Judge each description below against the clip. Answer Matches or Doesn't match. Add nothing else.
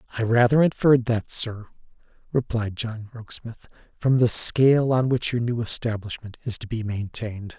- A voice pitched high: Doesn't match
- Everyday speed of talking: Matches